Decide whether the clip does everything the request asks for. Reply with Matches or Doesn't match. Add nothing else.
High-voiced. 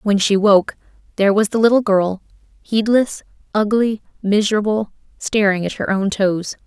Matches